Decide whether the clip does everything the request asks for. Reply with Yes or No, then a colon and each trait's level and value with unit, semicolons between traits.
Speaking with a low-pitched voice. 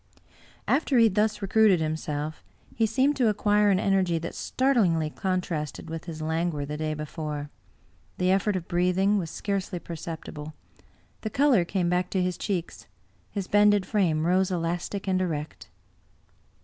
No: medium, 180 Hz